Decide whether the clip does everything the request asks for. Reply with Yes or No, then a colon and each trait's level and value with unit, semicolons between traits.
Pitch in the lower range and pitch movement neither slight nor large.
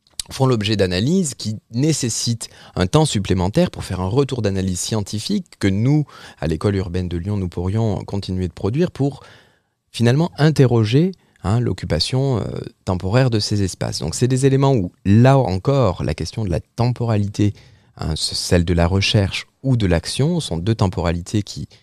No: low, 110 Hz; wide, 5.9 semitones